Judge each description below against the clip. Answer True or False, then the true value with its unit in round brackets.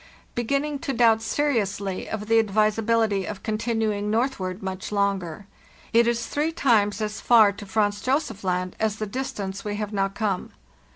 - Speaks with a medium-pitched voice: False (215 Hz)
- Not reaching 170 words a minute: True (160 wpm)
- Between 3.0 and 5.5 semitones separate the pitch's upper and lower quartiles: False (2.6 semitones)